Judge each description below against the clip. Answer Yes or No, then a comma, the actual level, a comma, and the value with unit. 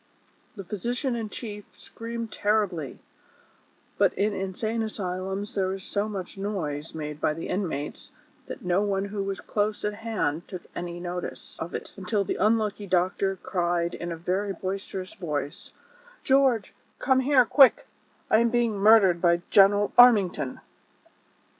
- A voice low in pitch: No, high, 195 Hz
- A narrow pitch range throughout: No, average, 3.4 semitones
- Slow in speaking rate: No, average, 145 wpm